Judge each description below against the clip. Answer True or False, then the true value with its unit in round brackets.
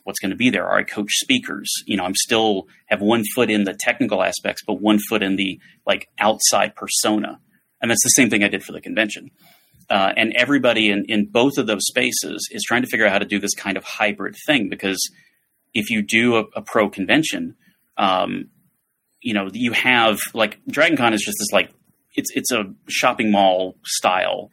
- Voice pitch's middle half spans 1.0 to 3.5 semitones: True (2.6 semitones)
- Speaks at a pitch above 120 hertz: False (105 Hz)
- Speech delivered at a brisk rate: True (210 wpm)